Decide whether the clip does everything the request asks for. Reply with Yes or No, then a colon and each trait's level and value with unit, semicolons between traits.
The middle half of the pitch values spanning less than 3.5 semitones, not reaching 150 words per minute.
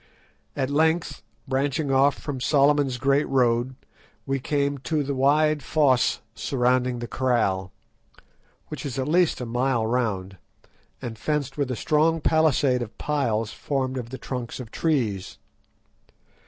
Yes: average, 3.0 semitones; average, 140 wpm